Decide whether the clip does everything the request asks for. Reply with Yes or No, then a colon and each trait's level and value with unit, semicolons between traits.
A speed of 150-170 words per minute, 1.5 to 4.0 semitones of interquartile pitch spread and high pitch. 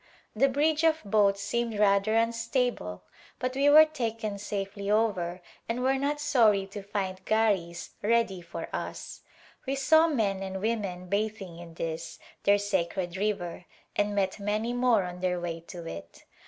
Yes: average, 155 wpm; average, 3.7 semitones; high, 205 Hz